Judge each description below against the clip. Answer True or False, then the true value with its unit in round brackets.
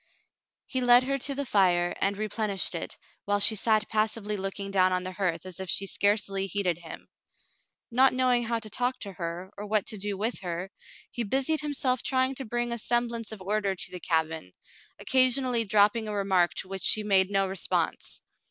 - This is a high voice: True (205 Hz)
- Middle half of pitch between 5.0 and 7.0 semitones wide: False (4.0 semitones)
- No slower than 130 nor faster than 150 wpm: False (195 wpm)